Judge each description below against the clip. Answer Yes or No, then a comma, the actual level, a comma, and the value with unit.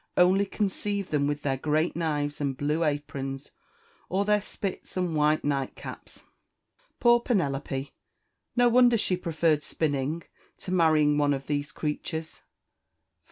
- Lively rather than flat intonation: No, average, 4.3 semitones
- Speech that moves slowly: Yes, slow, 130 wpm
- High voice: No, medium, 155 Hz